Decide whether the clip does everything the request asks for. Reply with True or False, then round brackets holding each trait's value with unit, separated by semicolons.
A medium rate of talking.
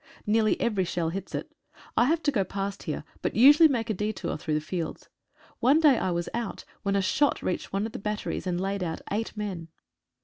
False (215 wpm)